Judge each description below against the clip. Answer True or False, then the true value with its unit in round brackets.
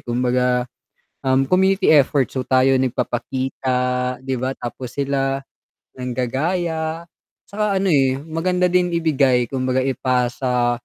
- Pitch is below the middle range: True (130 Hz)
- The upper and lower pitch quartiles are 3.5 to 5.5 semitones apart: True (4.0 semitones)